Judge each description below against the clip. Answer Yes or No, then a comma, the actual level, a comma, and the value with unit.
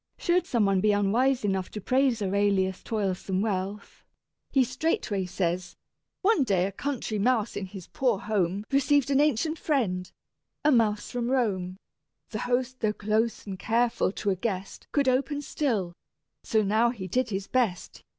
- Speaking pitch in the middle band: No, high, 215 Hz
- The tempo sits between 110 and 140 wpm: No, average, 160 wpm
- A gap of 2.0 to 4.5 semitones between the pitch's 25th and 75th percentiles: No, average, 4.9 semitones